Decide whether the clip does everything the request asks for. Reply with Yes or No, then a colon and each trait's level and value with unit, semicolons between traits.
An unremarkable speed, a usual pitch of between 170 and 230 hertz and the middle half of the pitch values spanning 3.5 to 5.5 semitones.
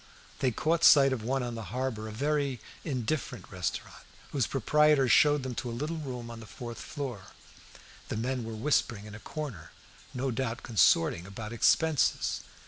No: average, 170 wpm; low, 125 Hz; average, 4.0 semitones